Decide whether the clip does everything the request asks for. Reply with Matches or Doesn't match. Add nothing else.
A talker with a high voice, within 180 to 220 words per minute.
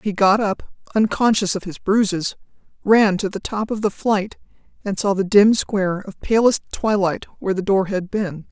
Matches